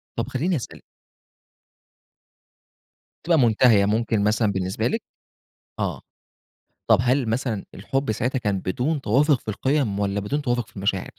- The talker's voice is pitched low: Yes, low, 115 Hz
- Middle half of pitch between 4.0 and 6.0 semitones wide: Yes, average, 4.8 semitones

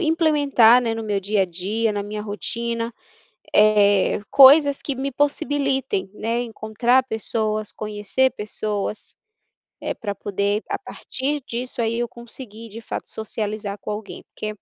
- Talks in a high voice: Yes, high, 225 Hz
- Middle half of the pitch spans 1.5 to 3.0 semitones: No, average, 3.5 semitones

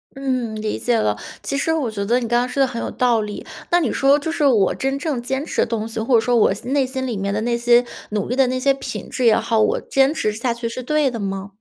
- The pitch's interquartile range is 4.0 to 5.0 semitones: No, average, 3.4 semitones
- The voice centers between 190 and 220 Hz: No, high, 245 Hz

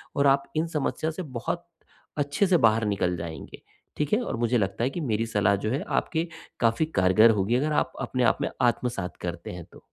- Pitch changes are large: Yes, wide, 6.9 semitones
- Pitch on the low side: Yes, low, 120 Hz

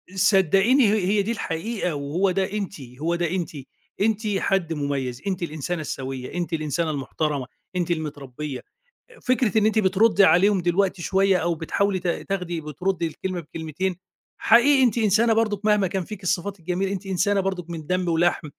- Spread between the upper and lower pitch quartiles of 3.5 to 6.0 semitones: Yes, average, 3.8 semitones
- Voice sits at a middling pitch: Yes, medium, 180 Hz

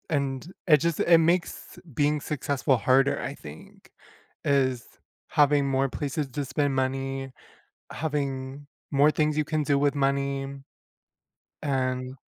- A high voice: No, medium, 140 Hz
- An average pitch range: No, narrow, 2.0 semitones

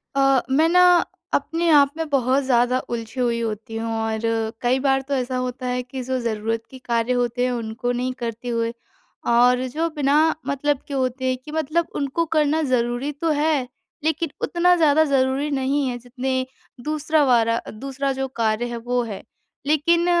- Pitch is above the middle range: Yes, very high, 260 Hz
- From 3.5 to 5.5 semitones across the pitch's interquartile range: No, average, 3.1 semitones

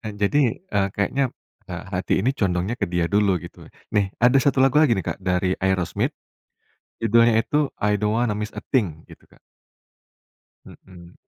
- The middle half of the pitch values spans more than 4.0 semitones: Yes, average, 4.4 semitones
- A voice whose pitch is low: Yes, low, 105 Hz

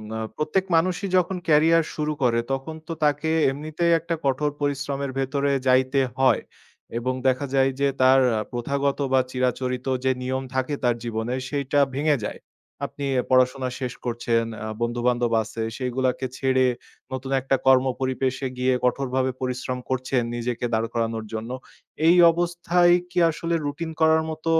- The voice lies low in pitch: Yes, low, 130 Hz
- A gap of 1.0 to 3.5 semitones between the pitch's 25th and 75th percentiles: Yes, average, 2.8 semitones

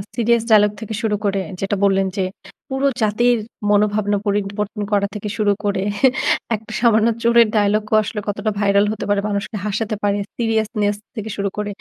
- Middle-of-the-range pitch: No, high, 210 Hz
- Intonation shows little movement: Yes, narrow, 1.4 semitones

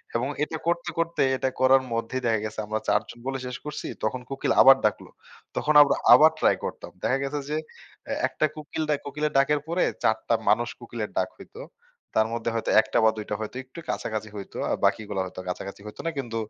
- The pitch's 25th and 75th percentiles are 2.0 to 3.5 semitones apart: No, average, 5.3 semitones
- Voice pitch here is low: Yes, low, 130 Hz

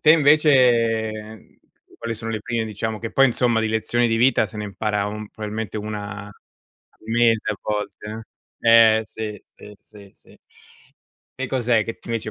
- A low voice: Yes, low, 110 Hz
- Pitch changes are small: Yes, narrow, 1.6 semitones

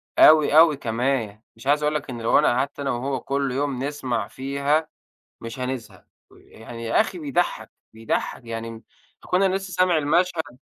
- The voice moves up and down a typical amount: Yes, average, 4.6 semitones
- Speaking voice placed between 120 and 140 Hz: Yes, low, 135 Hz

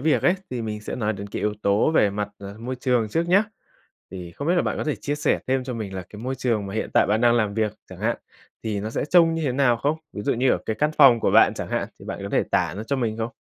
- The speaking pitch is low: Yes, low, 115 Hz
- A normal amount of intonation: Yes, average, 4.4 semitones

